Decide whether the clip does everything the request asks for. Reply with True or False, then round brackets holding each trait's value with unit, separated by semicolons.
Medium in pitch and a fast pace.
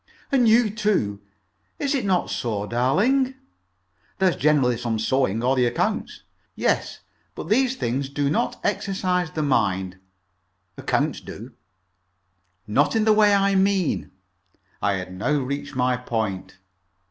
False (145 Hz; 135 wpm)